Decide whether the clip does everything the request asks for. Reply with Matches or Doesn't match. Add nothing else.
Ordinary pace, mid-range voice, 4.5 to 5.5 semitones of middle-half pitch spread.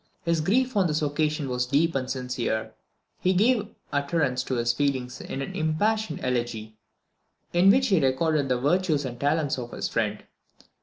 Matches